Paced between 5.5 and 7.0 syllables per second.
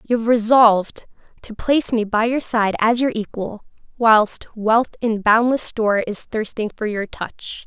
No: 4.4 syllables/s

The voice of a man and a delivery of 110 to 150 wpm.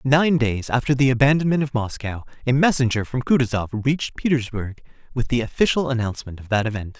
No: male; average, 170 wpm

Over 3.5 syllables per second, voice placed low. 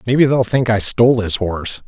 Yes: 5.8 syllables/s; low, 110 Hz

